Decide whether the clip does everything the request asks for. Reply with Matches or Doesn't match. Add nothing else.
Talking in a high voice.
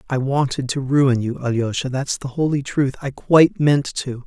Doesn't match